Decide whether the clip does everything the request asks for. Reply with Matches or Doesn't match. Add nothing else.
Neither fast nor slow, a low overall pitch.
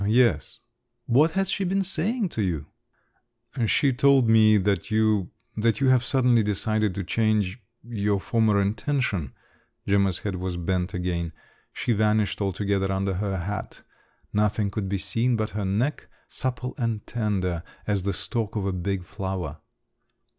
Matches